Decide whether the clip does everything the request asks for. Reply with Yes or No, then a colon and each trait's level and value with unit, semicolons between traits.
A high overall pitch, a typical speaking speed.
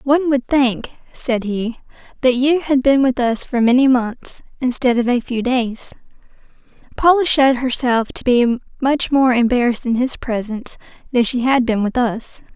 Yes: very high, 250 Hz; average, 170 wpm